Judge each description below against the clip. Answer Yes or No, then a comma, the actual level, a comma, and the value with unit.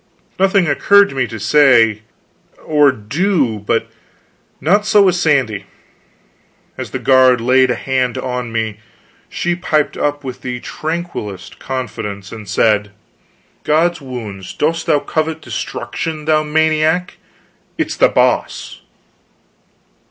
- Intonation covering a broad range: Yes, wide, 5.8 semitones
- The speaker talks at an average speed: No, slow, 125 wpm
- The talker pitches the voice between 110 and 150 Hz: Yes, low, 135 Hz